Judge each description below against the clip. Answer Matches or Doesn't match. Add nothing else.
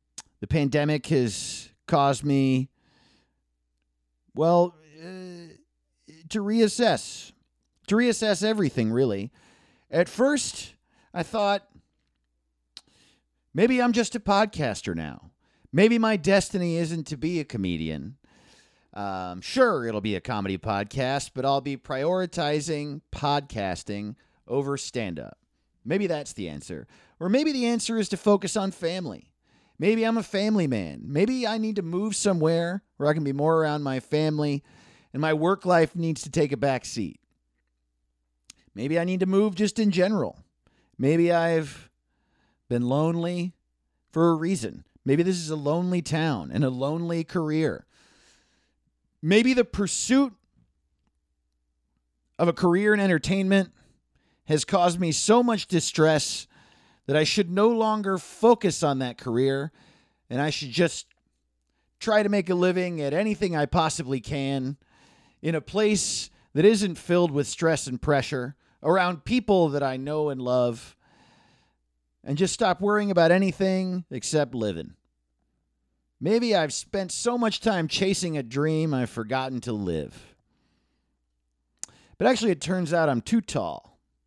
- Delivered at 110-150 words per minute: Matches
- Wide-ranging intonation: Matches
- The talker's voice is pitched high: Doesn't match